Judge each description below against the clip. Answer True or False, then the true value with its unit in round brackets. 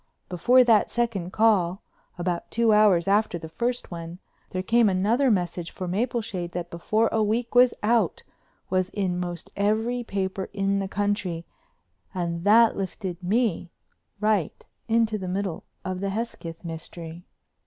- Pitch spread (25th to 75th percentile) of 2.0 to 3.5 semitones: False (4.0 semitones)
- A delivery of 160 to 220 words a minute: False (145 wpm)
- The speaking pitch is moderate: False (195 Hz)